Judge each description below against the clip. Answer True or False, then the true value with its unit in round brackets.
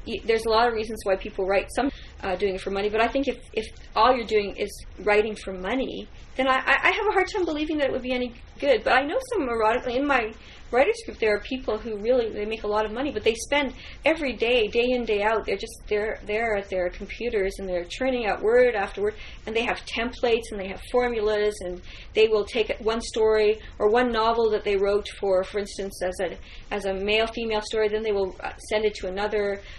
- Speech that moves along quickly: True (245 wpm)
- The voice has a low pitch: False (220 Hz)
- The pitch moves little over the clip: False (3.8 semitones)